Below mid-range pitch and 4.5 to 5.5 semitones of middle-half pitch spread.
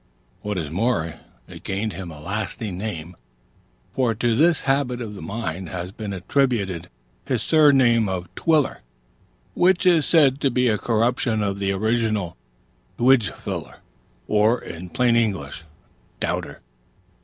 Yes: low, 110 Hz; average, 4.8 semitones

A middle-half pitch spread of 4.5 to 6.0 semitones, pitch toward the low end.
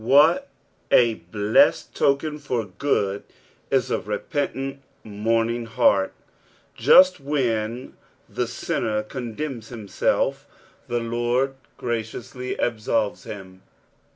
No: average, 4.0 semitones; low, 120 Hz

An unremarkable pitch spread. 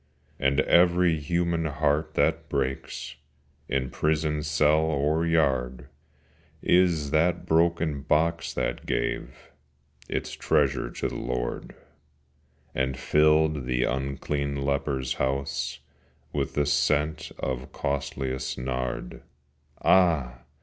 Yes: average, 3.0 semitones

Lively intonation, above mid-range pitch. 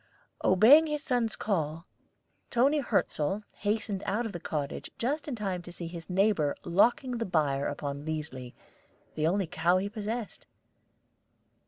Yes: wide, 6.4 semitones; high, 195 Hz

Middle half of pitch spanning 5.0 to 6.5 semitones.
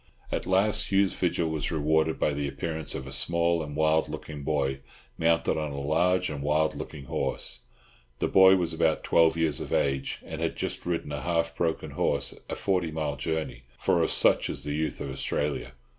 No: narrow, 2.6 semitones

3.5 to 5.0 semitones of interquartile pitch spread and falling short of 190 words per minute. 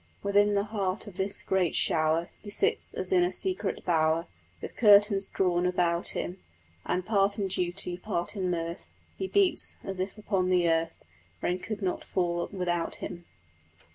No: average, 2.8 semitones; average, 170 wpm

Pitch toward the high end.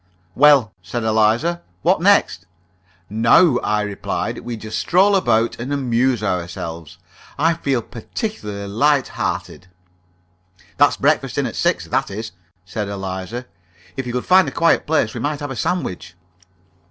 No: low, 115 Hz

